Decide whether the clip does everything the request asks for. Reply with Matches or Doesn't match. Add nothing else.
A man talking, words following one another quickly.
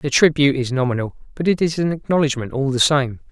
Matches